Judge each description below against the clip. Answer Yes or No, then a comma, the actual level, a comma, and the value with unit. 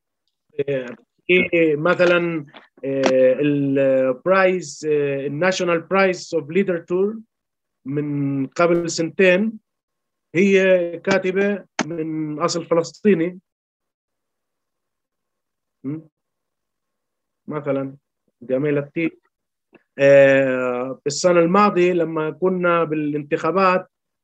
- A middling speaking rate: No, slow, 55 wpm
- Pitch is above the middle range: No, medium, 165 Hz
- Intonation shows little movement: No, average, 4.4 semitones